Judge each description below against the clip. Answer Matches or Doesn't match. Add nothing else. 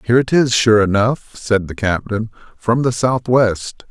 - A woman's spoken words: Doesn't match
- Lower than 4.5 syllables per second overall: Matches